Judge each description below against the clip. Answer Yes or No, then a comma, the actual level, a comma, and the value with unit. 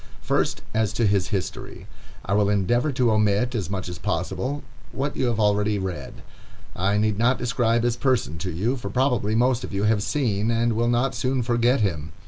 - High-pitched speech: No, low, 110 Hz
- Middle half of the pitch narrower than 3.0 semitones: No, average, 3.5 semitones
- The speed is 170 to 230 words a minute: Yes, average, 195 wpm